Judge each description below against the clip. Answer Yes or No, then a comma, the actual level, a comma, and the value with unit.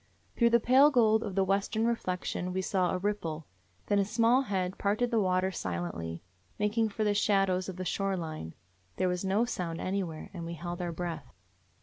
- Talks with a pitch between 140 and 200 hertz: Yes, high, 190 Hz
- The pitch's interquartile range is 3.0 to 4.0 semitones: Yes, average, 3.4 semitones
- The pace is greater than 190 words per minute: Yes, fast, 205 wpm